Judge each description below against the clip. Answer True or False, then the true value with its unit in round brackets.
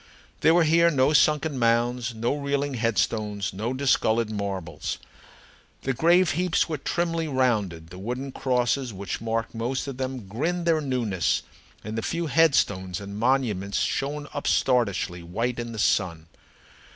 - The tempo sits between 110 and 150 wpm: True (145 wpm)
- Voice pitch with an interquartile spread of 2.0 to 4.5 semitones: False (5.3 semitones)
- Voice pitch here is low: True (125 Hz)